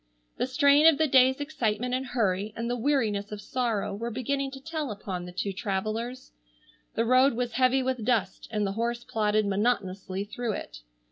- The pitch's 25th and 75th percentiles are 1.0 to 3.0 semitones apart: No, average, 4.0 semitones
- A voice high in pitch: Yes, high, 235 Hz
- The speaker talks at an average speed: Yes, average, 185 wpm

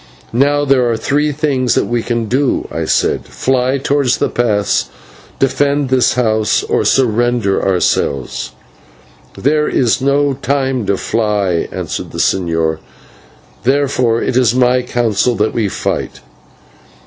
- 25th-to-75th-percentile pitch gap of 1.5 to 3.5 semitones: No, average, 3.9 semitones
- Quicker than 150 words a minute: No, slow, 135 wpm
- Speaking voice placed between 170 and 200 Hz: No, low, 125 Hz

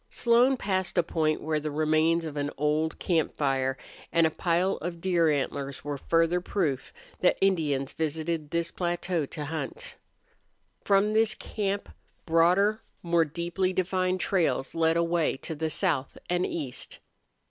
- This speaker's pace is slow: No, average, 145 wpm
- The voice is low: No, medium, 165 Hz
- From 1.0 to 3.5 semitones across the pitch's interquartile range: Yes, average, 3.1 semitones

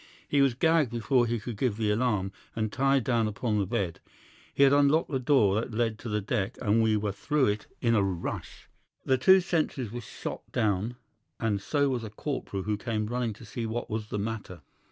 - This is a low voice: Yes, low, 115 Hz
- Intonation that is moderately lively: Yes, average, 3.7 semitones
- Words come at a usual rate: No, fast, 215 wpm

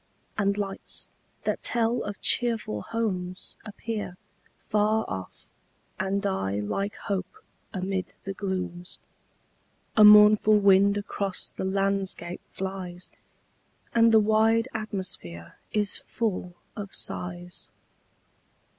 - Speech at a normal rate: No, slow, 100 wpm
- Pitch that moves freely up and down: No, average, 2.7 semitones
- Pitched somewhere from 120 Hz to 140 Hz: No, high, 195 Hz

